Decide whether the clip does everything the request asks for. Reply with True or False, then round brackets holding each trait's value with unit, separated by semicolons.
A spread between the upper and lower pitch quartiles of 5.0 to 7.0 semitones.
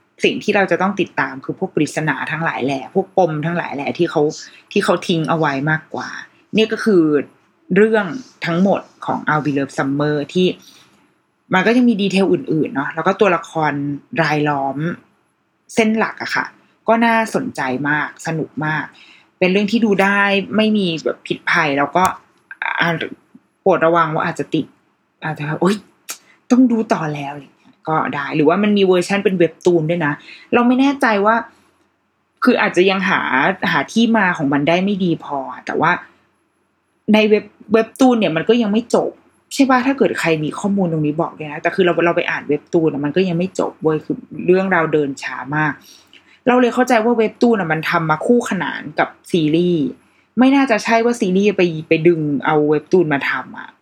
True (5.6 semitones)